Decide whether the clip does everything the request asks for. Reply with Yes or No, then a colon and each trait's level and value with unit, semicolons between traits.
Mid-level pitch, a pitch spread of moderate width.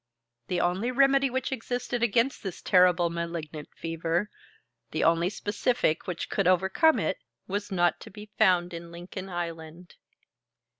Yes: medium, 180 Hz; average, 4.3 semitones